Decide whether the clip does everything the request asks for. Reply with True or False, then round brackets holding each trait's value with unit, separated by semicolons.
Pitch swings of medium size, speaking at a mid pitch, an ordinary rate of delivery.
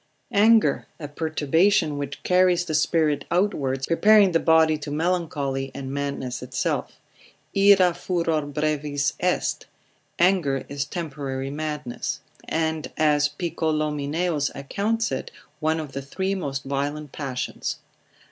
False (3.4 semitones; 155 Hz; 120 wpm)